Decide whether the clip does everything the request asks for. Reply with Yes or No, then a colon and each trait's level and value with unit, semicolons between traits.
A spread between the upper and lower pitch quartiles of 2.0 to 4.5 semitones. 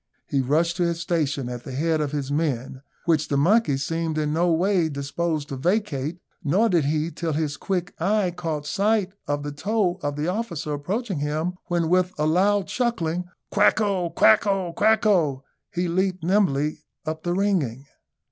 Yes: average, 4.2 semitones